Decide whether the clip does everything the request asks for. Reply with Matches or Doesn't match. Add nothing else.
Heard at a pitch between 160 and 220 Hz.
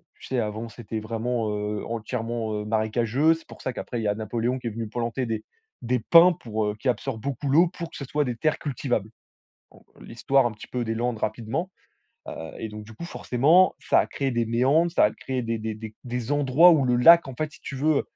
Doesn't match